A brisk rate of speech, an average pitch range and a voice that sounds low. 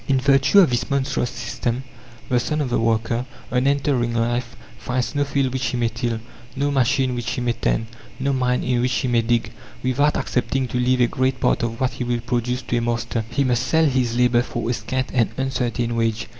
No: fast, 220 wpm; narrow, 1.8 semitones; low, 125 Hz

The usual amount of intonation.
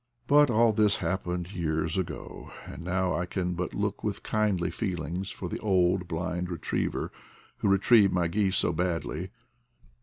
No: narrow, 2.3 semitones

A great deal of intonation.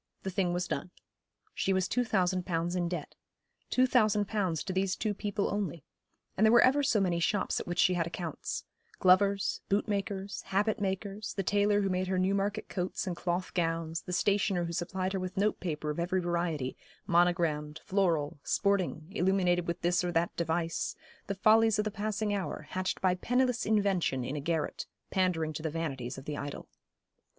No: average, 3.0 semitones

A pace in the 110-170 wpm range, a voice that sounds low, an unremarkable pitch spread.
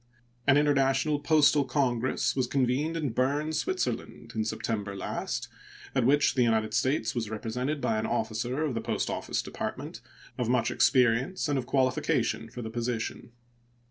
Yes: average, 155 wpm; low, 125 Hz; average, 3.9 semitones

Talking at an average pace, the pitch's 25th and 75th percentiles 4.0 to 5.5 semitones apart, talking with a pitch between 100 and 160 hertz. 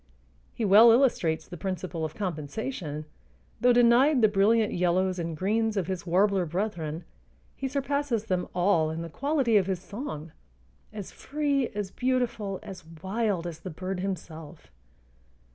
No: average, 145 wpm; average, 5.0 semitones; high, 195 Hz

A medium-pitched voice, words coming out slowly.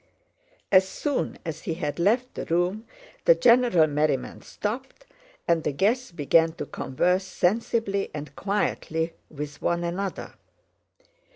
Yes: medium, 180 Hz; slow, 125 wpm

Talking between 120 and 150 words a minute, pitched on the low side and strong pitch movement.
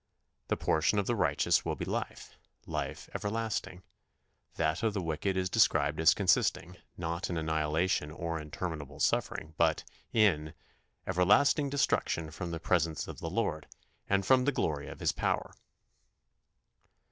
No: average, 145 wpm; very low, 85 Hz; average, 4.2 semitones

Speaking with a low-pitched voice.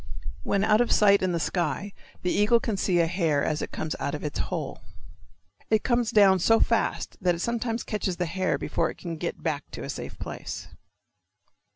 No: high, 190 Hz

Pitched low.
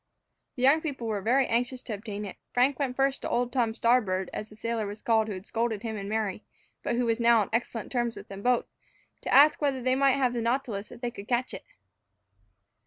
No: high, 235 Hz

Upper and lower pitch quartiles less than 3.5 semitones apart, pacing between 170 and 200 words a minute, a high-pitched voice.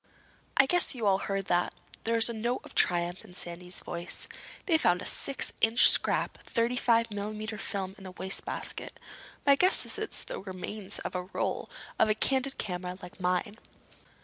No: average, 4.4 semitones; average, 185 wpm; high, 205 Hz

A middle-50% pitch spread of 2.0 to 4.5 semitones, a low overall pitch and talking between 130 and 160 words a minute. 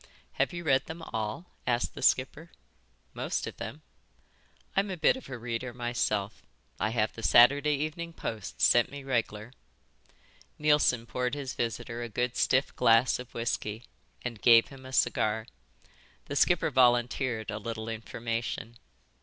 Yes: average, 3.2 semitones; low, 120 Hz; average, 150 wpm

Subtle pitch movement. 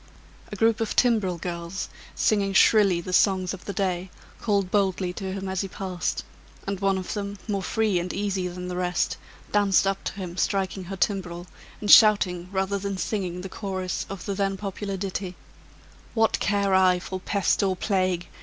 Yes: narrow, 1.7 semitones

